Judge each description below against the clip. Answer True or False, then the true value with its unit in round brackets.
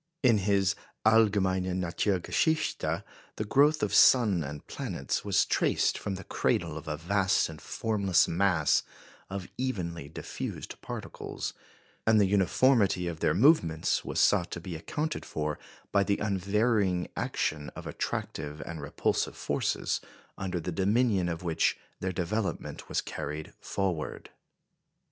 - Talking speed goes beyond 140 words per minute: False (135 wpm)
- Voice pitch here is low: True (95 Hz)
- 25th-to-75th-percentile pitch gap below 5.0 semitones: True (4.0 semitones)